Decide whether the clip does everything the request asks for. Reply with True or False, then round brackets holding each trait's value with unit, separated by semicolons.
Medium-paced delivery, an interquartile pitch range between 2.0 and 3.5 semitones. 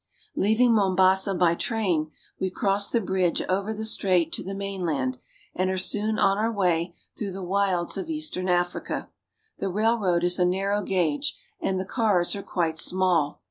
True (170 wpm; 2.4 semitones)